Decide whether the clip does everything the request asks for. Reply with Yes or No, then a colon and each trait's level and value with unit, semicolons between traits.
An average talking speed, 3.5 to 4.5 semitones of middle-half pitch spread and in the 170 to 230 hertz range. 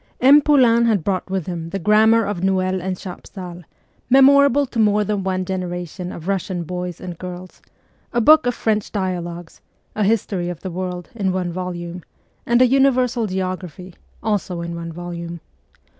Yes: average, 165 wpm; average, 3.8 semitones; medium, 185 Hz